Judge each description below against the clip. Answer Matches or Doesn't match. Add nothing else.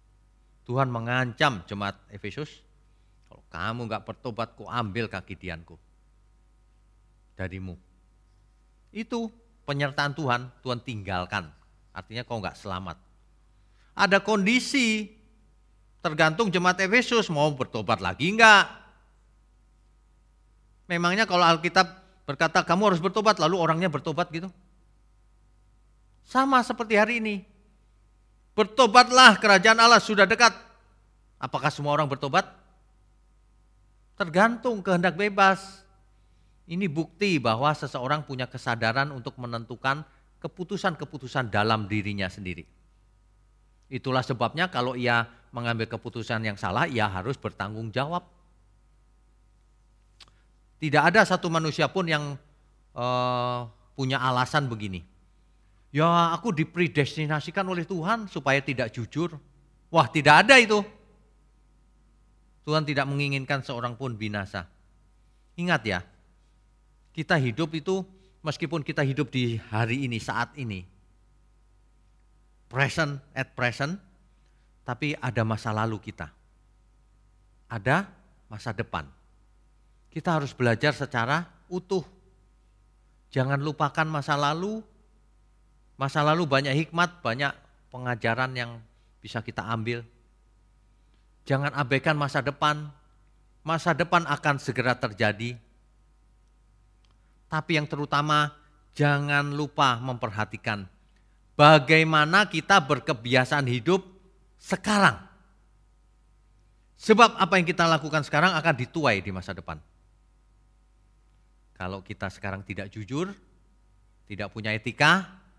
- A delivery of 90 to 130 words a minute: Matches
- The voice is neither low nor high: Doesn't match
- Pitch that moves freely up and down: Matches